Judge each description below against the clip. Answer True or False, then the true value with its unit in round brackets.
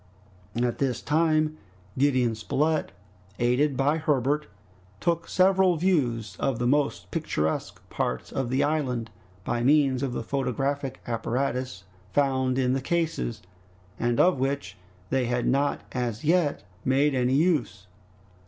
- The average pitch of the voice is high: False (135 Hz)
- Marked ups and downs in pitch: False (3.5 semitones)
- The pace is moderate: False (130 wpm)